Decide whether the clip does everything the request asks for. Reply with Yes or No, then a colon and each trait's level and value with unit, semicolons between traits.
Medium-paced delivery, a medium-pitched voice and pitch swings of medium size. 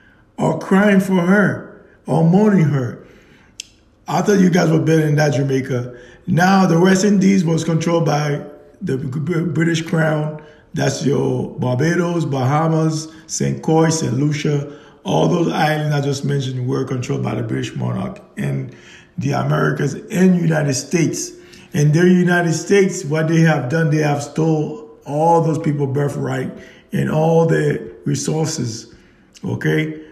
Yes: average, 145 wpm; medium, 155 Hz; average, 3.1 semitones